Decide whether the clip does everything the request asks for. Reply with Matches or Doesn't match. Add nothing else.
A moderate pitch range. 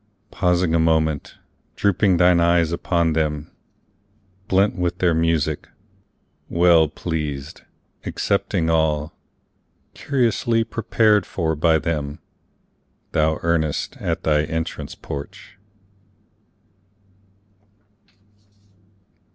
Doesn't match